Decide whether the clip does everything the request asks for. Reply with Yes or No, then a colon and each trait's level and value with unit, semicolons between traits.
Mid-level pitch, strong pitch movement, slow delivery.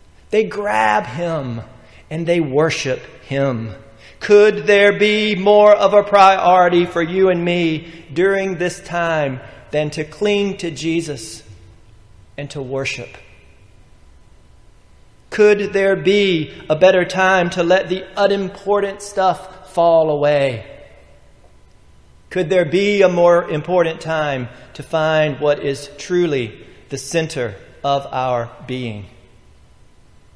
Yes: medium, 160 Hz; wide, 6.7 semitones; slow, 115 wpm